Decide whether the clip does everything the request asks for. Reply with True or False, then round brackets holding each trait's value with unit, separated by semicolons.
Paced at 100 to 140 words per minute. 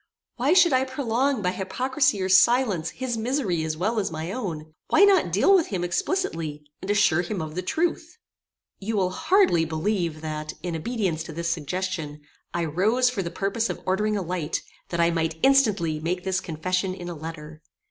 False (190 wpm)